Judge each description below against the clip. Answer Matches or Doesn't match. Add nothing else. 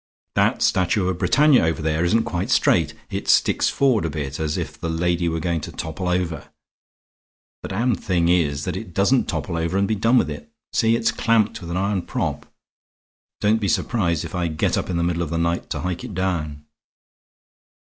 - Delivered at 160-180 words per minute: Doesn't match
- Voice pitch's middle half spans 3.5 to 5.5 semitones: Matches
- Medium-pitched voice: Doesn't match